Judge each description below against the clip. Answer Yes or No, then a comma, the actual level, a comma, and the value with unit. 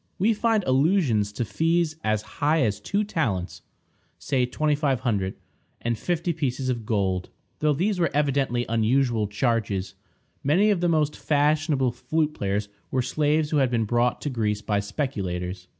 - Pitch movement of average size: No, wide, 6.3 semitones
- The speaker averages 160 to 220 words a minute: No, average, 150 wpm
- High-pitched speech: No, low, 130 Hz